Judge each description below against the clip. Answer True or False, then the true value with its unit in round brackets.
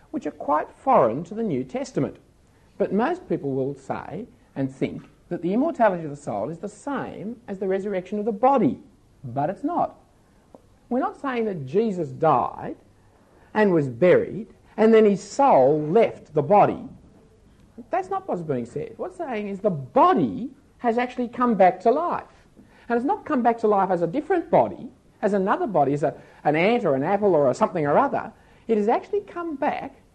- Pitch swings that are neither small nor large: False (6.1 semitones)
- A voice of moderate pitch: False (215 Hz)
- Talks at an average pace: True (190 wpm)